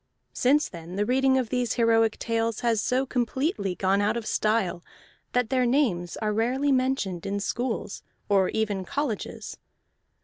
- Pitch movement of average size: Yes, average, 4.1 semitones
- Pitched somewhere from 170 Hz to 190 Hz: No, high, 225 Hz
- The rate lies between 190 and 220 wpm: No, average, 150 wpm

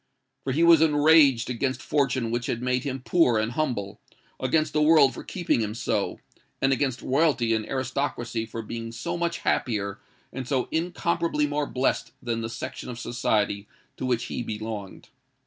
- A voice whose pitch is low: Yes, low, 130 Hz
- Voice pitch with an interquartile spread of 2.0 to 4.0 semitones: No, average, 4.5 semitones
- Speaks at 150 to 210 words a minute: Yes, average, 165 wpm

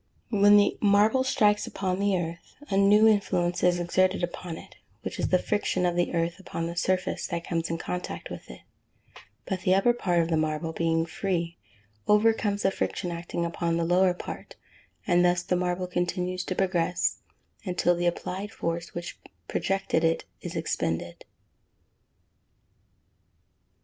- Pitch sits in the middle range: Yes, medium, 180 Hz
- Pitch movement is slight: Yes, narrow, 2.3 semitones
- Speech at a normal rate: Yes, average, 160 wpm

